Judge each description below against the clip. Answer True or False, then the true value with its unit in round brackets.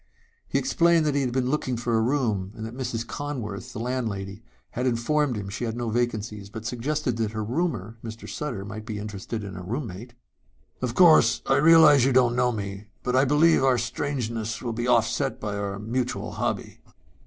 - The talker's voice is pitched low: True (120 Hz)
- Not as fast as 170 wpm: False (195 wpm)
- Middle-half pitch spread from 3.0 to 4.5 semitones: True (3.5 semitones)